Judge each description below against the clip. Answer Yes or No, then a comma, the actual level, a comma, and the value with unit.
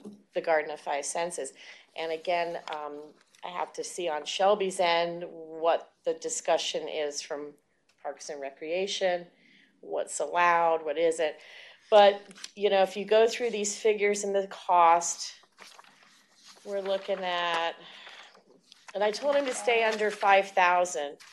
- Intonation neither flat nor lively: Yes, average, 3.8 semitones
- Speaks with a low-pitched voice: No, medium, 185 Hz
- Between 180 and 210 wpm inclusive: No, average, 140 wpm